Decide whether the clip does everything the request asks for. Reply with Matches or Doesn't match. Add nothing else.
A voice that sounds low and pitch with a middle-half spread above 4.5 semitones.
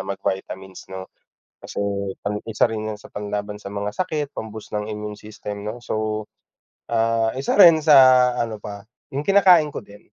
Doesn't match